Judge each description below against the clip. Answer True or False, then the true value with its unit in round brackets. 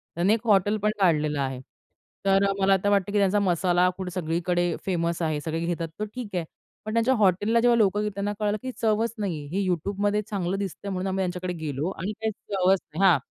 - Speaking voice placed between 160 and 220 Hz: True (190 Hz)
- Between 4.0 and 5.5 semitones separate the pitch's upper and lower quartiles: False (2.9 semitones)